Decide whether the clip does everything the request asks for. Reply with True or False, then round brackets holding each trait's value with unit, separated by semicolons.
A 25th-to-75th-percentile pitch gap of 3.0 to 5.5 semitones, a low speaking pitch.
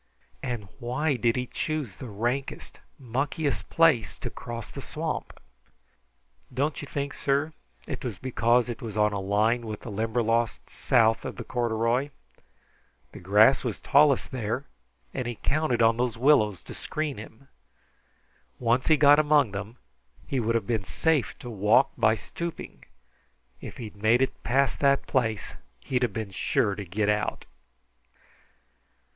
True (3.9 semitones; 120 Hz)